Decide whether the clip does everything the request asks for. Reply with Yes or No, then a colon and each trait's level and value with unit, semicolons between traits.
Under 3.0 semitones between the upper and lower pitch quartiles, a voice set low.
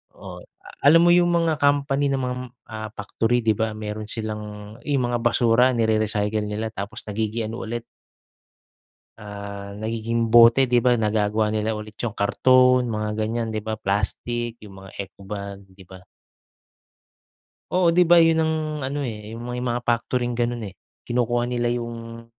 Yes: narrow, 2.4 semitones; low, 115 Hz